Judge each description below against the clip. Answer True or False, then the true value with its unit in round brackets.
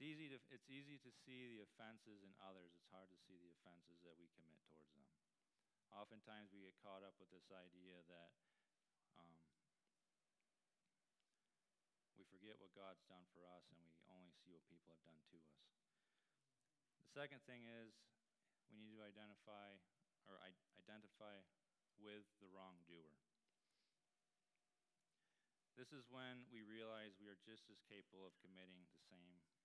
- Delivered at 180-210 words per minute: False (155 wpm)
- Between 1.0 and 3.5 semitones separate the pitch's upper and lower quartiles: False (3.9 semitones)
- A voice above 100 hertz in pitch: False (95 Hz)